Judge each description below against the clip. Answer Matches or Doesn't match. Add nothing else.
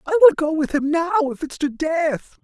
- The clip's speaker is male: Matches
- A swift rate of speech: Matches